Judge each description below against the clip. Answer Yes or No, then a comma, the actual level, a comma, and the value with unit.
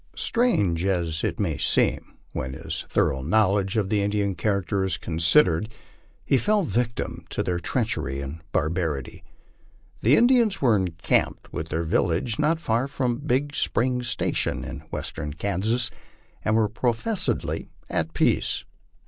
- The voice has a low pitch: Yes, low, 100 Hz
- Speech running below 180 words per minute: Yes, average, 145 wpm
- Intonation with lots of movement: Yes, wide, 7.0 semitones